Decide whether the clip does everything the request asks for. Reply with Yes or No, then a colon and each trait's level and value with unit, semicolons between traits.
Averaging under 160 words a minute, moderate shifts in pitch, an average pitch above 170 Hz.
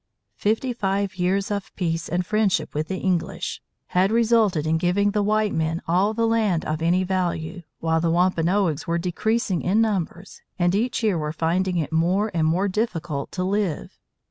No: average, 175 wpm; average, 3.7 semitones; medium, 185 Hz